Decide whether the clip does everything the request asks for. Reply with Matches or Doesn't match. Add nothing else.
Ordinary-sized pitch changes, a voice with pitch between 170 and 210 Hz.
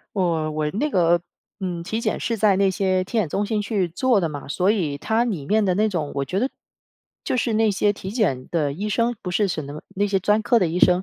Matches